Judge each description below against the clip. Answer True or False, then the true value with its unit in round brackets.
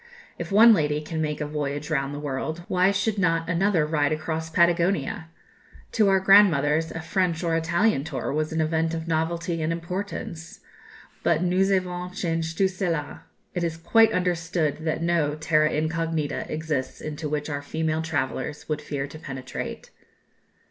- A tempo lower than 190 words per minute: True (160 wpm)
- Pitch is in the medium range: True (160 Hz)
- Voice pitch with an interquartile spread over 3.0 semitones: False (2.4 semitones)